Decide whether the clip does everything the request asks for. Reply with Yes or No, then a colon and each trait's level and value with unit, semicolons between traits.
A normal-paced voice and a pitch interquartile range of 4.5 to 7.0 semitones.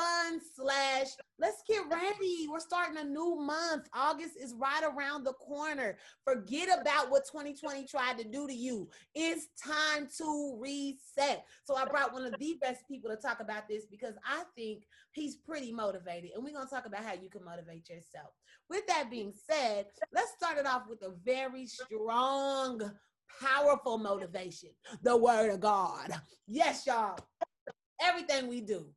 Yes: average, 165 wpm; average, 5.1 semitones